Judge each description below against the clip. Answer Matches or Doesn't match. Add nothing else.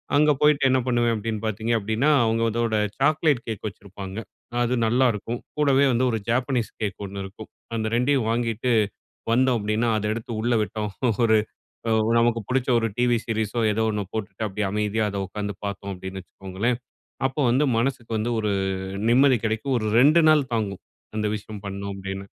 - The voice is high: Doesn't match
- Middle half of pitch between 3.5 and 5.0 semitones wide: Doesn't match